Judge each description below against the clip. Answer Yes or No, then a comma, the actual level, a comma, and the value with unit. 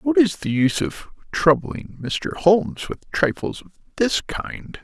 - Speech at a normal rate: Yes, average, 160 wpm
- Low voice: No, medium, 175 Hz